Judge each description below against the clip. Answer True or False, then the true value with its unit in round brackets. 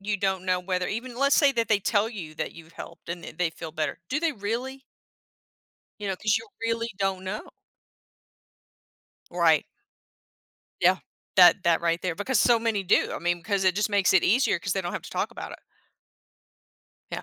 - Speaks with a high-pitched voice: True (195 Hz)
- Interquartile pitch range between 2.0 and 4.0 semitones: False (4.4 semitones)